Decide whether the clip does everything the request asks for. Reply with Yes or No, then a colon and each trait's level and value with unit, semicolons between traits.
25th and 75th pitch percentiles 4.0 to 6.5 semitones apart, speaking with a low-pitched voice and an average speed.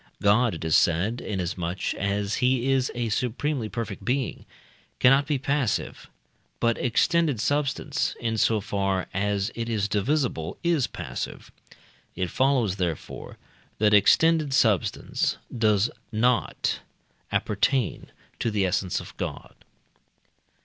No: average, 4.8 semitones; low, 115 Hz; slow, 115 wpm